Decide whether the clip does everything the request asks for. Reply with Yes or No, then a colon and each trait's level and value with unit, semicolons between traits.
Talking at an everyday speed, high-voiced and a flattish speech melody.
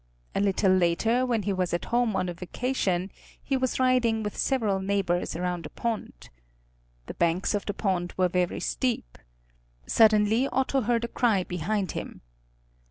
No: average, 165 wpm; high, 205 Hz; average, 4.6 semitones